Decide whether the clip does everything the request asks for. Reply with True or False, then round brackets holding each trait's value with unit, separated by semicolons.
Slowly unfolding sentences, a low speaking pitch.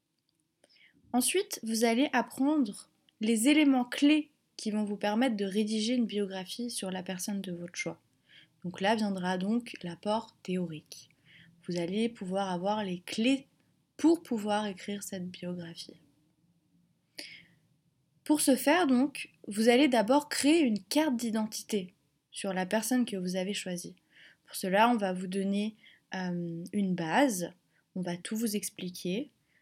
False (140 wpm; 205 Hz)